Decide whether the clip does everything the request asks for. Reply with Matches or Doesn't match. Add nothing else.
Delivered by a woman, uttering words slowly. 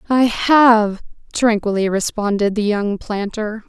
Matches